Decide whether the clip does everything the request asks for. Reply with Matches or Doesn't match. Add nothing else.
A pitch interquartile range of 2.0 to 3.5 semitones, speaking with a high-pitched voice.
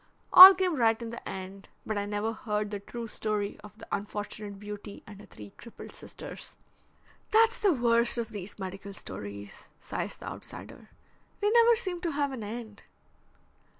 Doesn't match